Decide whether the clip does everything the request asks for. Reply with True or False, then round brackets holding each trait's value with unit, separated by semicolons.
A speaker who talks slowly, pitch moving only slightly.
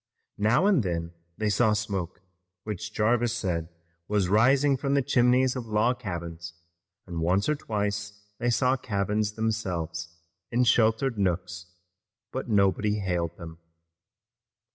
False (130 wpm; 4.9 semitones)